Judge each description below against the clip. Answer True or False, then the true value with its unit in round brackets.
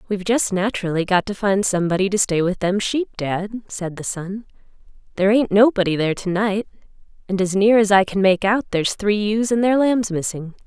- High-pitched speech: True (200 Hz)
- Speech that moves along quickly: True (210 wpm)